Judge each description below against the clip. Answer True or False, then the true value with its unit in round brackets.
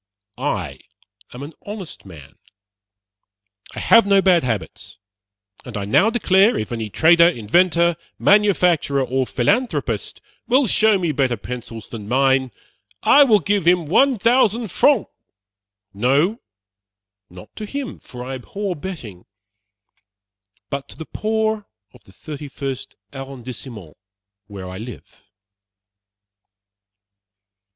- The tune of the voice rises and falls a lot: True (8.8 semitones)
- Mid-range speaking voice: True (145 Hz)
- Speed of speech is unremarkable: False (115 wpm)